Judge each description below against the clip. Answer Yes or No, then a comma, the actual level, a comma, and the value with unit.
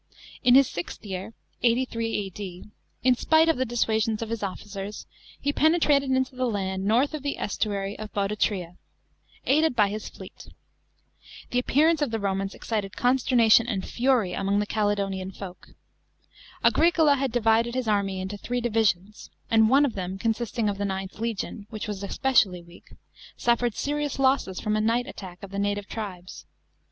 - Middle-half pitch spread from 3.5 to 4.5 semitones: Yes, average, 4.1 semitones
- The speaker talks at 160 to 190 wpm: Yes, average, 165 wpm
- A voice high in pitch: Yes, high, 220 Hz